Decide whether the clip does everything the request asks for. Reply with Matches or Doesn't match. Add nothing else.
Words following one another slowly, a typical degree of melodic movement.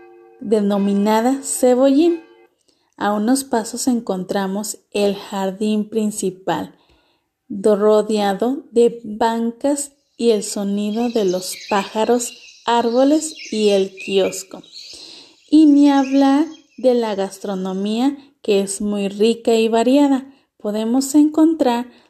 Matches